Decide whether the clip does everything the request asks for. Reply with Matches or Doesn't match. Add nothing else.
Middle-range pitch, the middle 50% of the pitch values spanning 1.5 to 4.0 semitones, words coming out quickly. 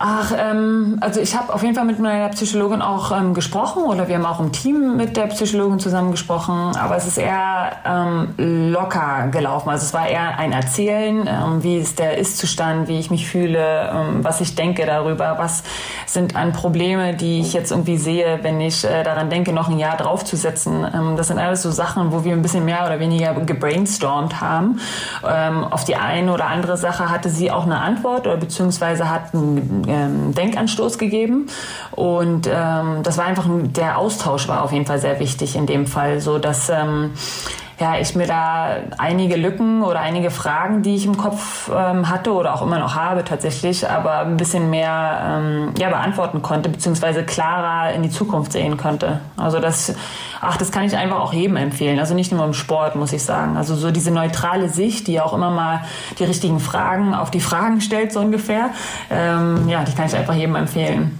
Matches